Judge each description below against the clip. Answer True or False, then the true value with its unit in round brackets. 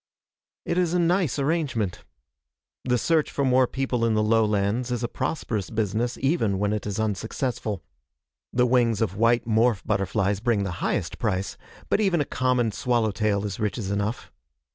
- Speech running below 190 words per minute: True (165 wpm)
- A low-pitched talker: True (115 Hz)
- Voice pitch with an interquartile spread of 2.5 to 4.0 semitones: True (3.6 semitones)